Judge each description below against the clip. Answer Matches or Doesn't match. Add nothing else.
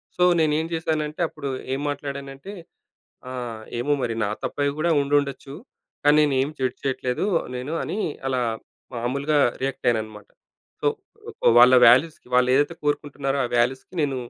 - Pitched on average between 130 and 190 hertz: Matches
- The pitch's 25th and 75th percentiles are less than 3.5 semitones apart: Matches